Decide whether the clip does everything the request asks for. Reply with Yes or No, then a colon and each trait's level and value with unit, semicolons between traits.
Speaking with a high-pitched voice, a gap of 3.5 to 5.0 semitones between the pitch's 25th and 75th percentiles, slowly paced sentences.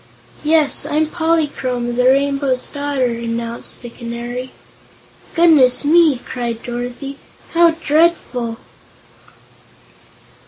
Yes: very high, 260 Hz; average, 4.1 semitones; slow, 85 wpm